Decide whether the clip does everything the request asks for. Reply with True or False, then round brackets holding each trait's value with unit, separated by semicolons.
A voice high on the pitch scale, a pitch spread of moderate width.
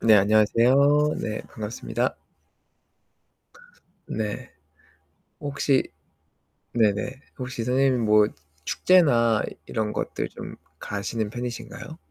False (115 Hz; 3.8 semitones)